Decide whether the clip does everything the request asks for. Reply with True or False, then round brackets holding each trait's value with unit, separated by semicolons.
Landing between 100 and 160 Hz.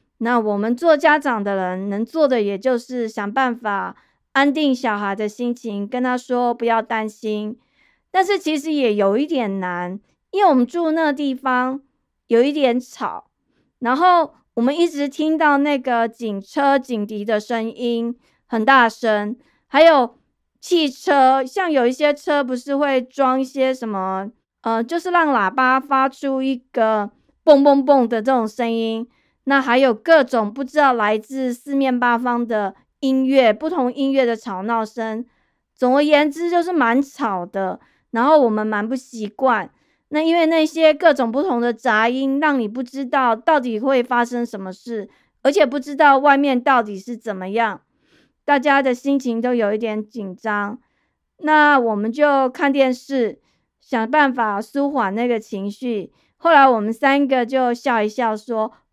False (250 Hz)